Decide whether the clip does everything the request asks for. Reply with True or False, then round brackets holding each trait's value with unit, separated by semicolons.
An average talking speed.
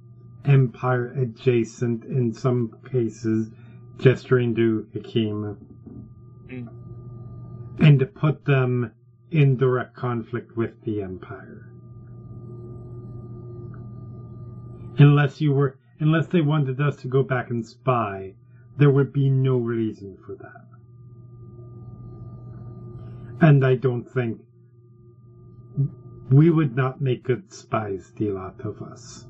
False (105 wpm)